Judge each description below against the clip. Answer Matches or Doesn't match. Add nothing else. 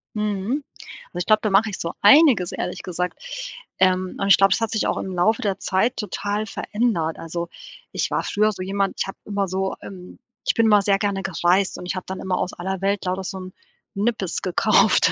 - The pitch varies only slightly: Matches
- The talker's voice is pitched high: Matches